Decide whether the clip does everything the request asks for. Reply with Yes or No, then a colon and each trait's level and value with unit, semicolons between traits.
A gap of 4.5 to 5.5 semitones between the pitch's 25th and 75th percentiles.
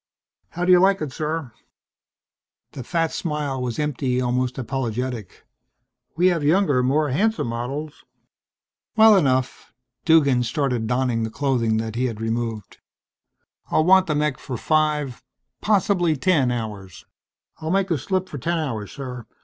Yes: average, 4.9 semitones